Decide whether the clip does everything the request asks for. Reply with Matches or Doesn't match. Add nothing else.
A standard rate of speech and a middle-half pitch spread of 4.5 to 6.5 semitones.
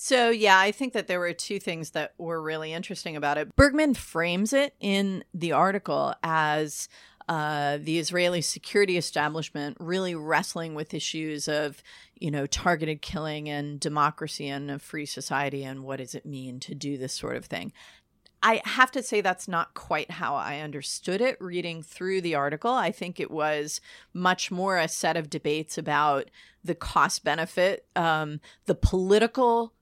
Doesn't match